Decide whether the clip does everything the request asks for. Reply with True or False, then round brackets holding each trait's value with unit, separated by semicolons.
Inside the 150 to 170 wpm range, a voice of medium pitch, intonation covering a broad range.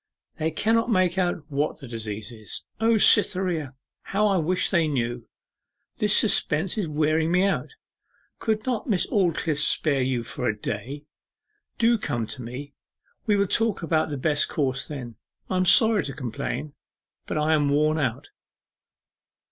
True (160 wpm; 155 Hz; 6.2 semitones)